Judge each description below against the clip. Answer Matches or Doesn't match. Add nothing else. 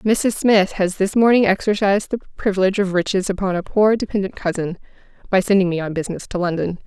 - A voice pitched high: Matches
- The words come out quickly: Doesn't match